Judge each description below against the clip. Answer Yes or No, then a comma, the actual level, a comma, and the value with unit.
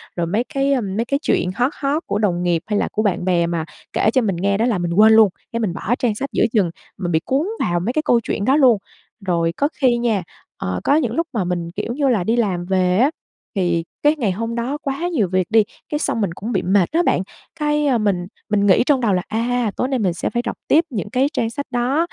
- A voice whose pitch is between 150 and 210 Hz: No, high, 220 Hz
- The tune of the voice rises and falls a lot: Yes, wide, 6.0 semitones